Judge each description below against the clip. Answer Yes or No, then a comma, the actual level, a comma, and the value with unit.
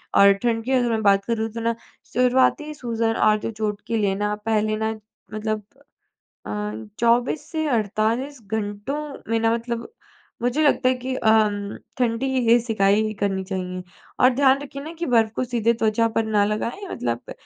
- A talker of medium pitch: No, high, 225 Hz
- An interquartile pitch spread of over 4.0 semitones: No, average, 2.8 semitones